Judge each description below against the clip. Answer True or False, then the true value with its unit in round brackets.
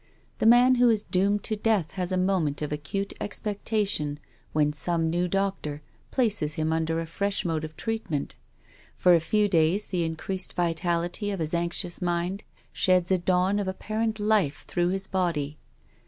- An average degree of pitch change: True (3.9 semitones)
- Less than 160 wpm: False (170 wpm)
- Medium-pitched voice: True (180 Hz)